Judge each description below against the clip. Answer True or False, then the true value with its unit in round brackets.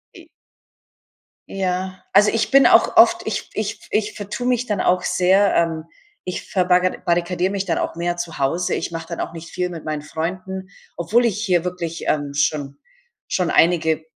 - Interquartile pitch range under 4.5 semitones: True (2.5 semitones)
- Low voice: False (180 Hz)